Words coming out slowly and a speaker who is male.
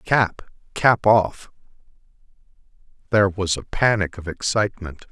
Yes: slow, 105 wpm; male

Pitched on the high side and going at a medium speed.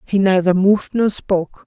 Yes: high, 195 Hz; average, 180 wpm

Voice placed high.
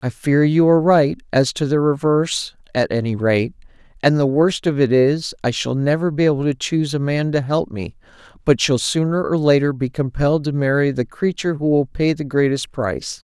No: medium, 140 Hz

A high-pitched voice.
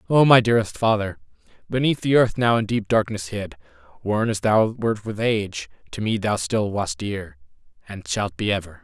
No: low, 110 Hz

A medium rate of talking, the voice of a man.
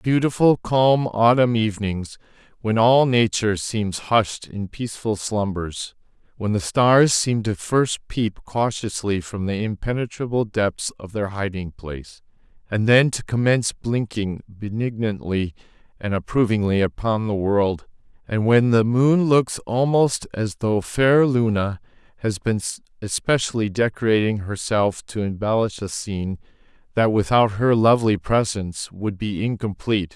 No: slow, 130 wpm; male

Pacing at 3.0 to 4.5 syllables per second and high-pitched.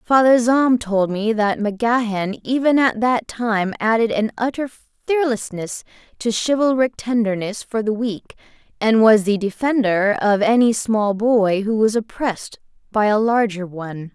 Yes: 4.4 syllables/s; high, 220 Hz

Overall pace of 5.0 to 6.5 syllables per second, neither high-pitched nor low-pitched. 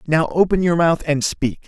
No: 4.8 syllables/s; medium, 160 Hz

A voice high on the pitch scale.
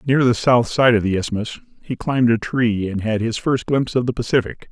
No: low, 120 Hz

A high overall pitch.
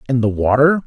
No: low, 130 Hz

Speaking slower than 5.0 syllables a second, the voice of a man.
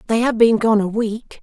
No: 4.8 syllables/s; female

